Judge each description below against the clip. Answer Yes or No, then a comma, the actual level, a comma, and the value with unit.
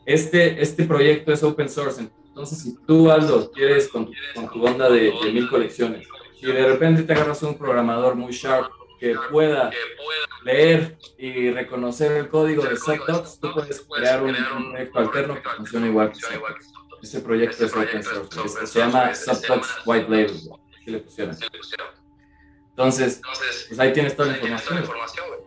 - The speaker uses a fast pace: No, average, 160 wpm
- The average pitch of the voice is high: No, low, 130 Hz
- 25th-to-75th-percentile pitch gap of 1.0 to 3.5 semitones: No, average, 4.2 semitones